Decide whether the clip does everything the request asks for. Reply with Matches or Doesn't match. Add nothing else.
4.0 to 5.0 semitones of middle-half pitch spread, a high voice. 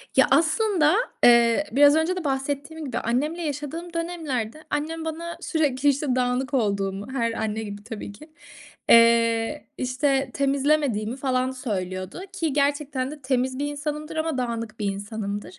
Matches